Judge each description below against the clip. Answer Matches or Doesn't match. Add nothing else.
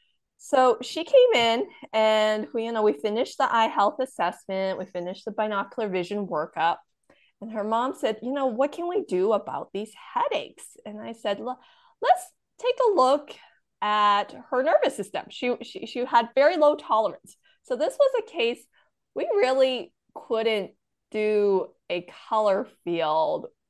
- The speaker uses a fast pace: Doesn't match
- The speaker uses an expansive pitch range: Matches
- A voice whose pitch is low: Doesn't match